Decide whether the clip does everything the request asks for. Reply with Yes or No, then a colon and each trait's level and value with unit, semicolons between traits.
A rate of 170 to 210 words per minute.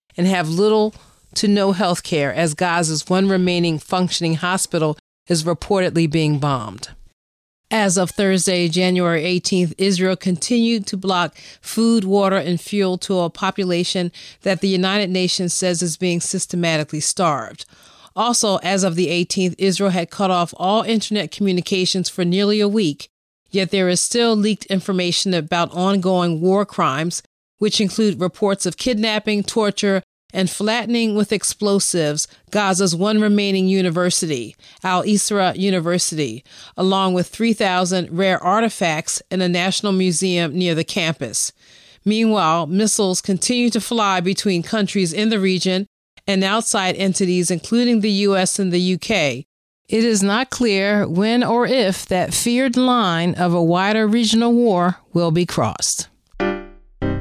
No: average, 140 wpm